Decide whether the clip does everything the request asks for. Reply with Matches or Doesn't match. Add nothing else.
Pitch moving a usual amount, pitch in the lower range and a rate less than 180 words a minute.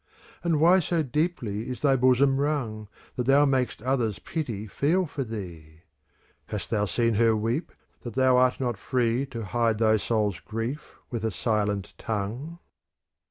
Matches